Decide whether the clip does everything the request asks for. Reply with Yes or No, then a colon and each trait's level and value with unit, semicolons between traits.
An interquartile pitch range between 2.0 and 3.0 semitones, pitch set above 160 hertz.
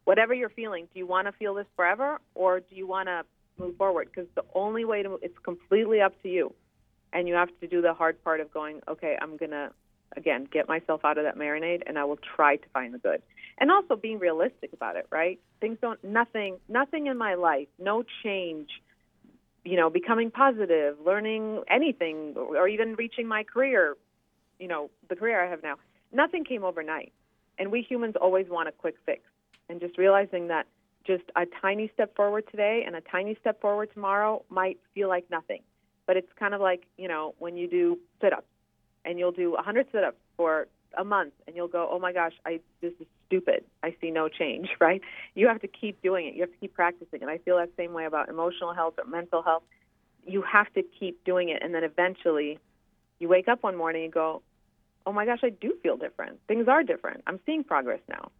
No: average, 4.2 semitones; medium, 185 Hz